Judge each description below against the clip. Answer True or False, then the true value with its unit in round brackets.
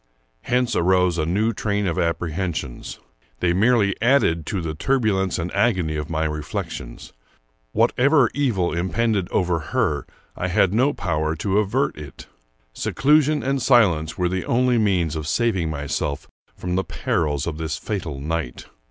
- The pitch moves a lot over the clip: True (6.0 semitones)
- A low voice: True (90 Hz)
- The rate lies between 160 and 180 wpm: False (150 wpm)